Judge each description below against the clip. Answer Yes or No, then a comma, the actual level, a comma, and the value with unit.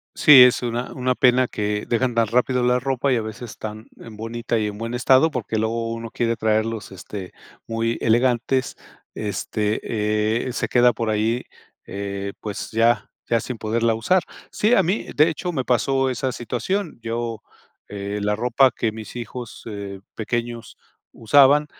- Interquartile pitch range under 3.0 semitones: Yes, narrow, 2.5 semitones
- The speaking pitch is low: Yes, low, 115 Hz